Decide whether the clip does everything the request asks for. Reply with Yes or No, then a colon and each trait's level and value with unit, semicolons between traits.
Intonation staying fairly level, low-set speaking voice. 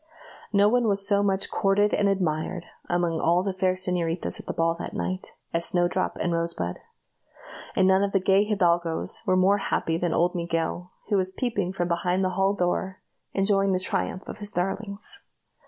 No: narrow, 2.3 semitones; medium, 185 Hz